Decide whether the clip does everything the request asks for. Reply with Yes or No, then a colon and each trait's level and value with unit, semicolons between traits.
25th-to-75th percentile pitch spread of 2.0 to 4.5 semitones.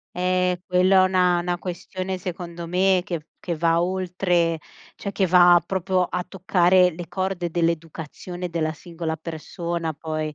No: narrow, 1.5 semitones